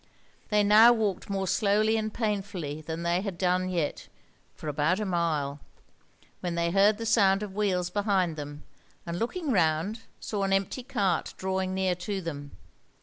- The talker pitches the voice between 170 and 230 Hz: Yes, high, 190 Hz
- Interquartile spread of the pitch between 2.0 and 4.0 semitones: Yes, average, 3.6 semitones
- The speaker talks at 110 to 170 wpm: Yes, average, 165 wpm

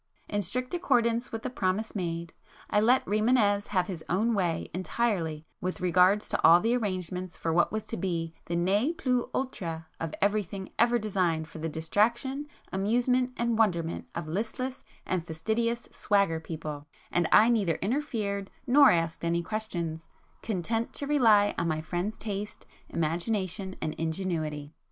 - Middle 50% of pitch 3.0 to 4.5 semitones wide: No, average, 5.3 semitones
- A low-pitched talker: No, high, 195 Hz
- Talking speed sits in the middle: Yes, average, 155 wpm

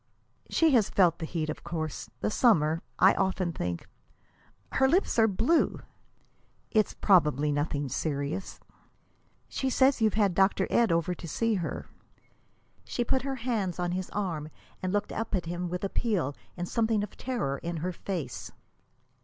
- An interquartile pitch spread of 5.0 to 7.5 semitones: Yes, average, 5.3 semitones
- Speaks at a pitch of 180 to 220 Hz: Yes, medium, 185 Hz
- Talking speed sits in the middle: Yes, average, 160 wpm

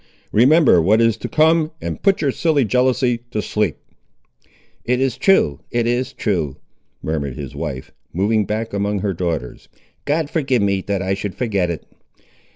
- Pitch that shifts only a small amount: No, wide, 5.5 semitones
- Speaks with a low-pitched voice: Yes, low, 110 Hz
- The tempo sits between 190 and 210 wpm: No, average, 165 wpm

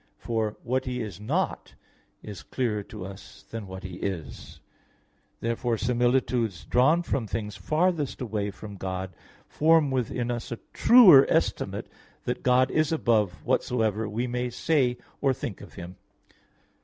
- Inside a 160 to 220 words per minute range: No, average, 145 wpm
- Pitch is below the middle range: Yes, low, 120 Hz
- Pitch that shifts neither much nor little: Yes, average, 4.0 semitones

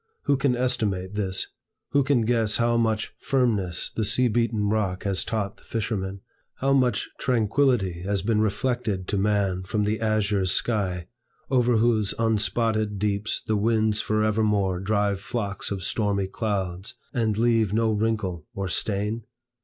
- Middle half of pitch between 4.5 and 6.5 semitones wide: No, narrow, 2.6 semitones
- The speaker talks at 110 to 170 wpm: Yes, average, 145 wpm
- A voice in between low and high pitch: No, low, 105 Hz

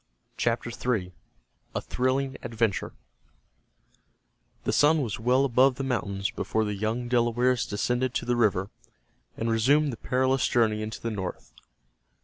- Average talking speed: No, slow, 130 wpm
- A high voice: No, low, 120 Hz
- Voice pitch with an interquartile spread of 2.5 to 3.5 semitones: Yes, average, 2.9 semitones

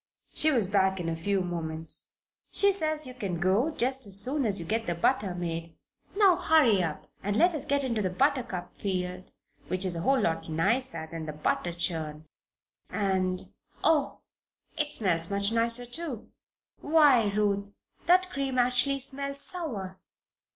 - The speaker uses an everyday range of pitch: No, wide, 7.2 semitones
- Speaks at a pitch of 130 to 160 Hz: No, high, 205 Hz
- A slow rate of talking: No, average, 165 wpm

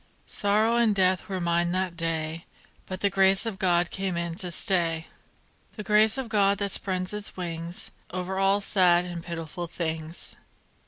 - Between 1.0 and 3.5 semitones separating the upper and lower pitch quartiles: Yes, average, 2.7 semitones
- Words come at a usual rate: Yes, average, 165 wpm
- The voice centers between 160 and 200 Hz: Yes, medium, 185 Hz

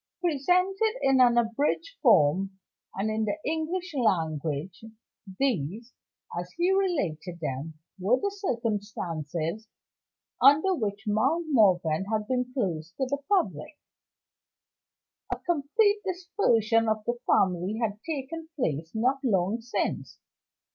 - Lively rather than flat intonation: Yes, wide, 8.5 semitones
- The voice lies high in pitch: Yes, high, 230 Hz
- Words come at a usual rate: No, slow, 115 wpm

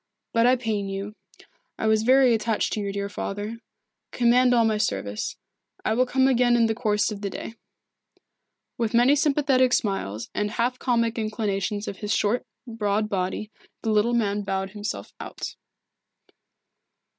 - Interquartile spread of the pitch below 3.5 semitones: Yes, average, 2.8 semitones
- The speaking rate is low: No, average, 160 wpm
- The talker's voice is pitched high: Yes, high, 220 Hz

